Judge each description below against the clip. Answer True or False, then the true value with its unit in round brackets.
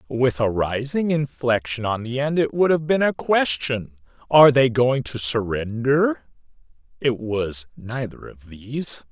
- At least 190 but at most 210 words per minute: False (150 wpm)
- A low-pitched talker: True (125 Hz)